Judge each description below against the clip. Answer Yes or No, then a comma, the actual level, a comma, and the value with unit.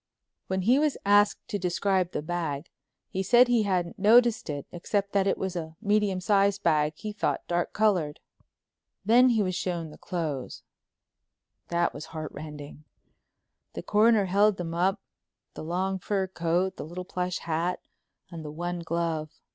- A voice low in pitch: No, medium, 180 Hz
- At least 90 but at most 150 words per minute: No, average, 165 wpm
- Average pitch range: Yes, average, 3.4 semitones